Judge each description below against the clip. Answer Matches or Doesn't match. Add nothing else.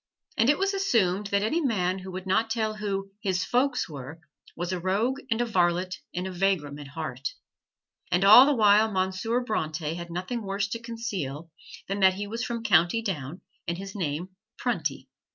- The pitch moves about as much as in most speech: Matches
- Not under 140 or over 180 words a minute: Doesn't match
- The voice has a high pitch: Matches